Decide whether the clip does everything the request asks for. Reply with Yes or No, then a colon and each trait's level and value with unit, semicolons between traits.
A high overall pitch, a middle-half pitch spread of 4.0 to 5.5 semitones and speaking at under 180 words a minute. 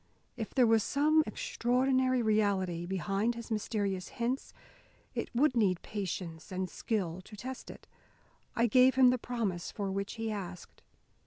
Yes: high, 220 Hz; average, 4.5 semitones; average, 150 wpm